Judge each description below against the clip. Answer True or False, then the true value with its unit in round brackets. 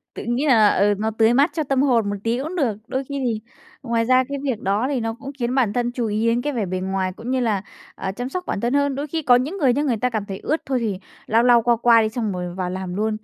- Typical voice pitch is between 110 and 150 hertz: False (235 Hz)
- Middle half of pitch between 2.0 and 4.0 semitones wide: True (3.7 semitones)